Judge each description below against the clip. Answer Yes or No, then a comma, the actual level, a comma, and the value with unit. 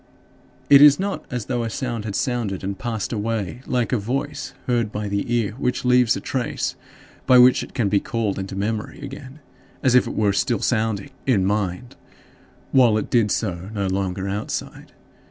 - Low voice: Yes, low, 115 Hz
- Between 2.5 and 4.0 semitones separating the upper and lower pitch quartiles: Yes, average, 3.7 semitones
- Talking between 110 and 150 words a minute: No, average, 185 wpm